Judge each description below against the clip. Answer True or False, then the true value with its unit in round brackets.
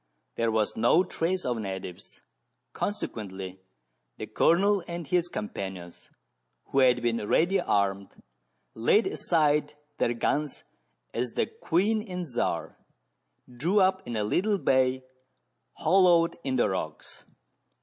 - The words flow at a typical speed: False (125 wpm)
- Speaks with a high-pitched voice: False (130 Hz)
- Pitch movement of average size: False (8.3 semitones)